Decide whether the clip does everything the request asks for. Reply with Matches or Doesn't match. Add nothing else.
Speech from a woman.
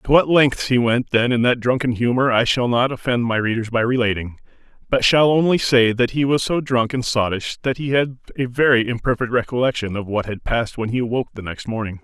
Doesn't match